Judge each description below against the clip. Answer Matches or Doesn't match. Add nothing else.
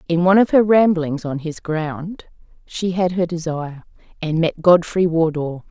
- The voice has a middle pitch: Matches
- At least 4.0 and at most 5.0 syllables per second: Matches